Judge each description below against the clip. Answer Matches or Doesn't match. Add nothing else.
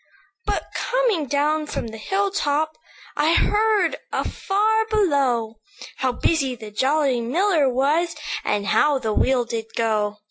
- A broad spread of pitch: Matches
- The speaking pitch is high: Matches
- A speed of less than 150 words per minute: Matches